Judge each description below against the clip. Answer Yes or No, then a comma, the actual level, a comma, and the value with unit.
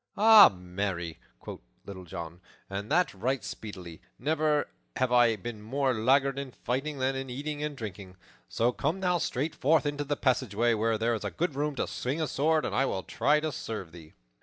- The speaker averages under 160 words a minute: No, average, 190 wpm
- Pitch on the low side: Yes, low, 130 Hz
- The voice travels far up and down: Yes, wide, 5.9 semitones